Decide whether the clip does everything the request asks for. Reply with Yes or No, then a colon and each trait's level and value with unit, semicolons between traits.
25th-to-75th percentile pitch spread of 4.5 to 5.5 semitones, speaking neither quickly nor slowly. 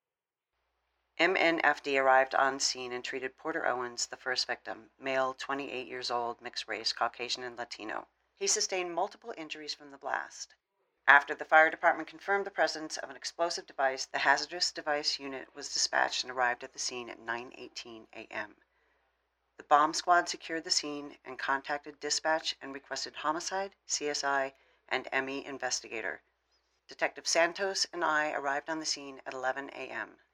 No: average, 3.3 semitones; average, 155 wpm